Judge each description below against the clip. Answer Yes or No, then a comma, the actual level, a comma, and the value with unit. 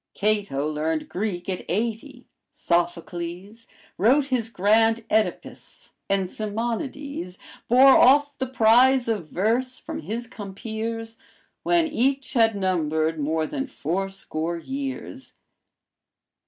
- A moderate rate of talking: No, slow, 110 wpm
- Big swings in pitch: Yes, wide, 6.1 semitones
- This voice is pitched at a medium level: No, high, 220 Hz